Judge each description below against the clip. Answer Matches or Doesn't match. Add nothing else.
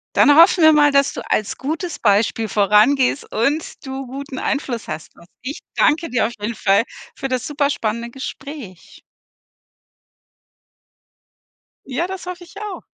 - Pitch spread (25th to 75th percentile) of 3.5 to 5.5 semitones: Matches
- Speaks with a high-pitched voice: Matches